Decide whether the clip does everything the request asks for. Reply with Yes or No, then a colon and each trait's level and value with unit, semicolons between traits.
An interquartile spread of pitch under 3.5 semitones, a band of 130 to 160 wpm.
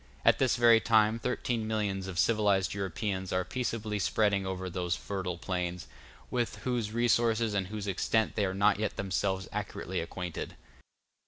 Yes: average, 3.0 semitones; average, 155 wpm